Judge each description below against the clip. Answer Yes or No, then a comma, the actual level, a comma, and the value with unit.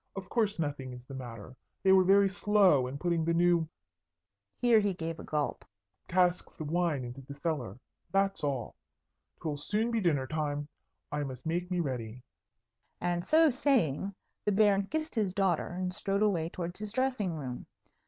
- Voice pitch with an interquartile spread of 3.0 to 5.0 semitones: No, wide, 5.6 semitones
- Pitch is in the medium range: Yes, medium, 175 Hz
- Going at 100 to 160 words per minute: No, average, 175 wpm